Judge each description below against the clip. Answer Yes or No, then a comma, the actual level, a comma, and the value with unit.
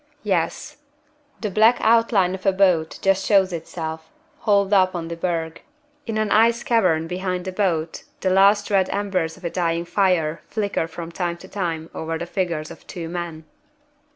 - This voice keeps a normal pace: Yes, average, 175 wpm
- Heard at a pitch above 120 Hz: Yes, medium, 185 Hz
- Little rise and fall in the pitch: No, average, 3.2 semitones